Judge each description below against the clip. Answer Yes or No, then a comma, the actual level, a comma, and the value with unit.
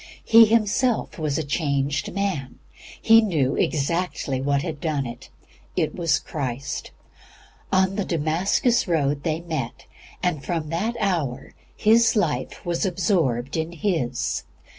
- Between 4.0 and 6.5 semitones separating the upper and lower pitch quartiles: Yes, average, 5.2 semitones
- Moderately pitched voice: Yes, medium, 165 Hz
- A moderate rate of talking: No, slow, 130 wpm